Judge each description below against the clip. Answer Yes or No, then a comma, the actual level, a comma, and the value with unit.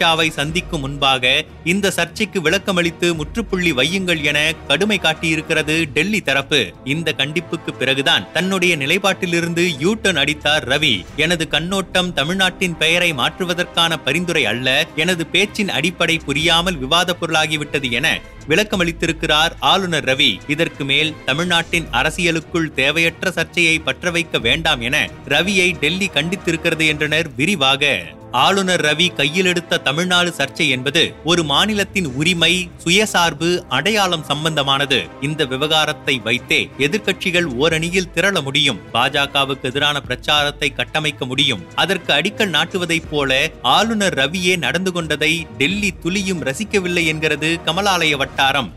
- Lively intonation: No, average, 3.6 semitones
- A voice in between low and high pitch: Yes, medium, 165 Hz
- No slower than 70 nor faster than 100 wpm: No, average, 110 wpm